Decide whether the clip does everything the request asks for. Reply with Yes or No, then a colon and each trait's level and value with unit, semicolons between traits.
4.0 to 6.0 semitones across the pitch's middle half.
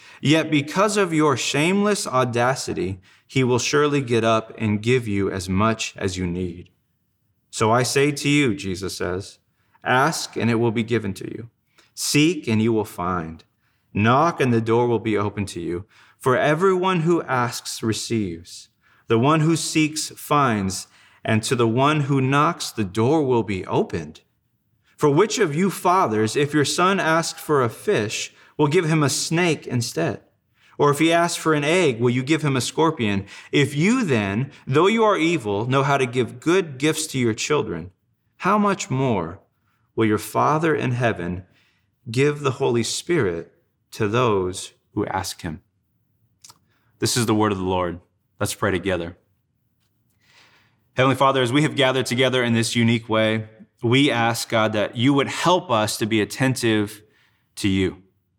Yes: wide, 5.6 semitones